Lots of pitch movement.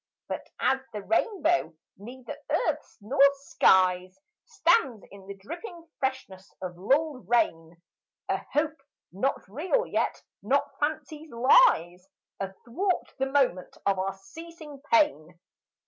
Yes: wide, 8.4 semitones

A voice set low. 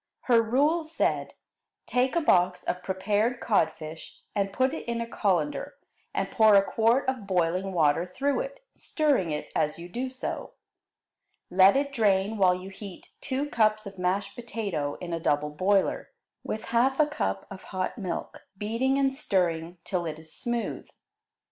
No: high, 200 Hz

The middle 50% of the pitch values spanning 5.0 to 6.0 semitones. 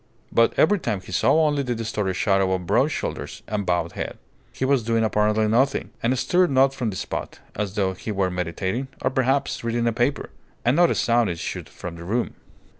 Yes: average, 5.3 semitones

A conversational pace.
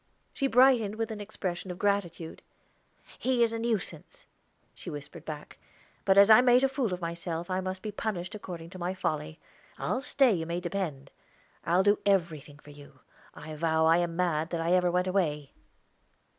Yes: average, 185 wpm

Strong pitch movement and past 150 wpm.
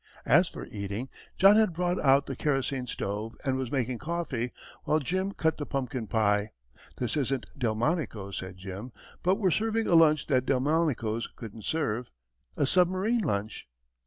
Yes: wide, 6.6 semitones; average, 160 wpm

